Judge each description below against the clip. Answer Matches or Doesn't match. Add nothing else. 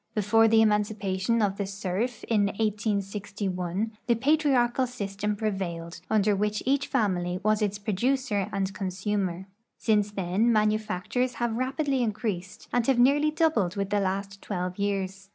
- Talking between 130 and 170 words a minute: Matches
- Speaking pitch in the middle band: Doesn't match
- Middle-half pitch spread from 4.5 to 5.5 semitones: Doesn't match